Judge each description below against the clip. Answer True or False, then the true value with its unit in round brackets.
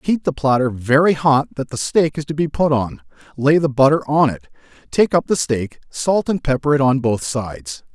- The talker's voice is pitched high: False (140 Hz)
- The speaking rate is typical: False (220 wpm)